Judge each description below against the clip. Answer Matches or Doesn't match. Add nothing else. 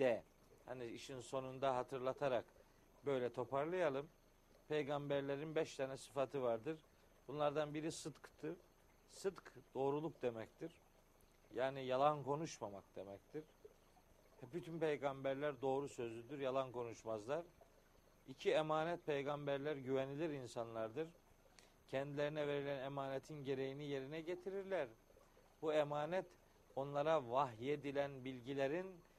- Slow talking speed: Matches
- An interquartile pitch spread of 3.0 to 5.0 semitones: Doesn't match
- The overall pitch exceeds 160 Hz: Doesn't match